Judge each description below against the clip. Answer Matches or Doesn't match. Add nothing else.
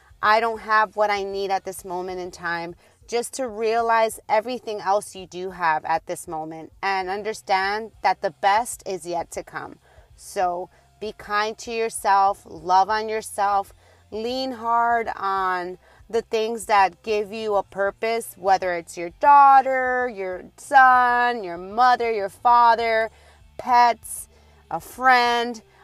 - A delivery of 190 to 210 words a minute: Doesn't match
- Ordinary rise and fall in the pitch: Matches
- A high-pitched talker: Matches